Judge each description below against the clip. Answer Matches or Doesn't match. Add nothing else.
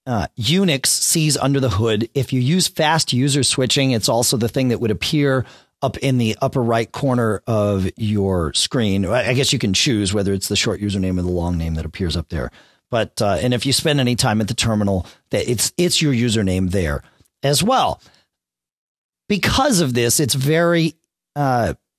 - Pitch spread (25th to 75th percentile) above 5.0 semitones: Matches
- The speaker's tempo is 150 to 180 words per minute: Doesn't match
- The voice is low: Matches